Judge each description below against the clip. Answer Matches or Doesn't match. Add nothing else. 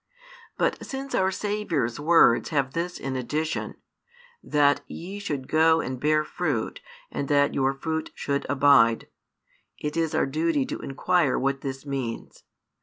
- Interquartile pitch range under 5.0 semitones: Matches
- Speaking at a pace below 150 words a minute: Matches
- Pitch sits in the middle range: Matches